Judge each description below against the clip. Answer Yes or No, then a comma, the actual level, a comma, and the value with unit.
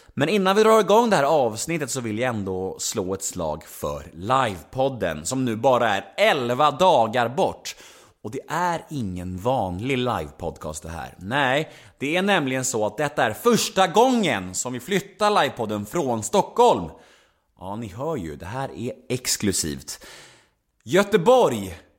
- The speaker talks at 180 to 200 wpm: No, average, 155 wpm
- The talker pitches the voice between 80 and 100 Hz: No, low, 130 Hz